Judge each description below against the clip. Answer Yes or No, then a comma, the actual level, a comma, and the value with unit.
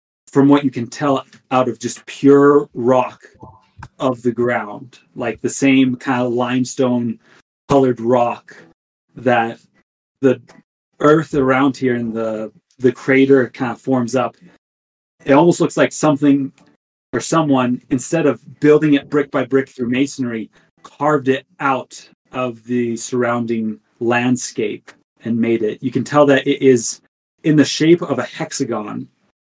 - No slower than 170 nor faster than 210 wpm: No, average, 145 wpm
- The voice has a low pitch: Yes, low, 130 Hz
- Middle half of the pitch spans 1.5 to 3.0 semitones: Yes, average, 2.7 semitones